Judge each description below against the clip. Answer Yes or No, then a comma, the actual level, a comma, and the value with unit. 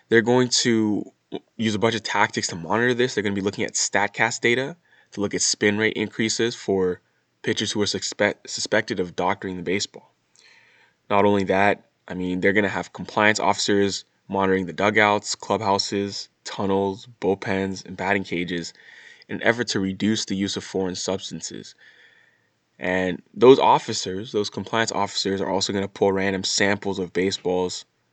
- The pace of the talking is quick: No, average, 170 wpm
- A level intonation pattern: Yes, narrow, 2.1 semitones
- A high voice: No, low, 100 Hz